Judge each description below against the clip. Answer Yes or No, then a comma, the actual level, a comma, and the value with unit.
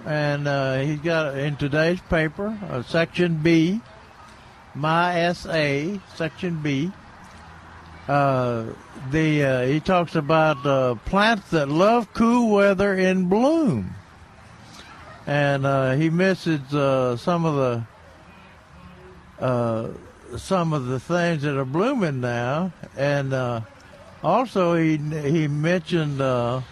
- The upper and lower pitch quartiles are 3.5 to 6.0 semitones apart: Yes, wide, 5.4 semitones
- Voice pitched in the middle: Yes, medium, 150 Hz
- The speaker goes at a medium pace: No, slow, 120 wpm